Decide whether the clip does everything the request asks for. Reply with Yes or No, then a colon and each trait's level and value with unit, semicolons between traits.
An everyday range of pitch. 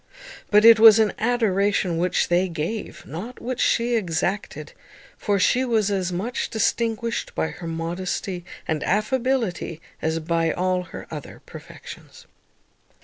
Yes: average, 4.7 semitones